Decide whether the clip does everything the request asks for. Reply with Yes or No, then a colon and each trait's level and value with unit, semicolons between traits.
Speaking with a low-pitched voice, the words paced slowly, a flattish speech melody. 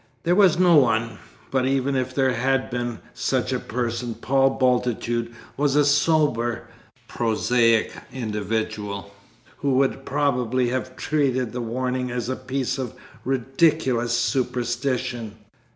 Yes: low, 125 Hz; slow, 125 wpm; narrow, 2.3 semitones